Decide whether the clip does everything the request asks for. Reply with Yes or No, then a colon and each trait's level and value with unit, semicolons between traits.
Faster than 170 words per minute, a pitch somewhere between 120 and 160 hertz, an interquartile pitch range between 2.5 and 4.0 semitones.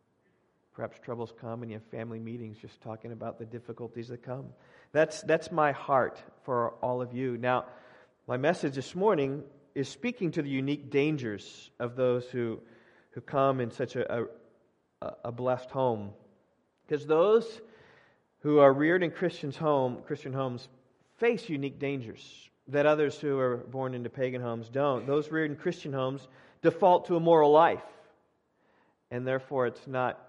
No: average, 160 wpm; low, 135 Hz; average, 3.6 semitones